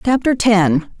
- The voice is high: Yes, high, 215 Hz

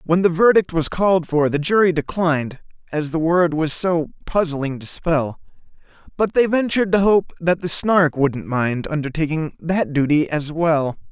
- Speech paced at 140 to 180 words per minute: Yes, average, 175 wpm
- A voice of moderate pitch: Yes, medium, 165 Hz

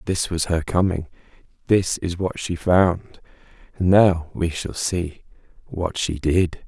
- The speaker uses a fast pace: No, average, 145 wpm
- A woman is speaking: No, male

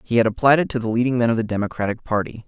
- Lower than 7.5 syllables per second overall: No, 7.6 syllables/s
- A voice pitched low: Yes, low, 115 Hz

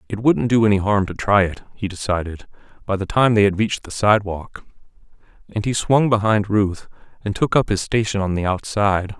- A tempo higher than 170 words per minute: Yes, average, 200 wpm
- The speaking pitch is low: Yes, low, 105 Hz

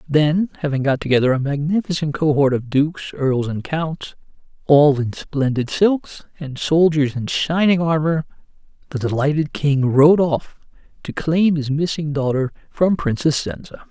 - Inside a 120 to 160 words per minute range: Yes, average, 145 wpm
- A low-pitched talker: No, medium, 150 Hz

